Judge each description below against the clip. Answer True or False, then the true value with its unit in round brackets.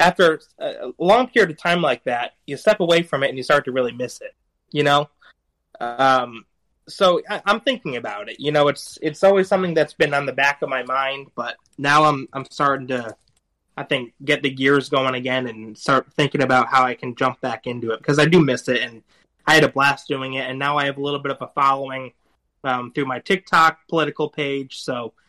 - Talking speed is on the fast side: True (230 wpm)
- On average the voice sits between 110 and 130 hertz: False (140 Hz)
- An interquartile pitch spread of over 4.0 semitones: False (2.7 semitones)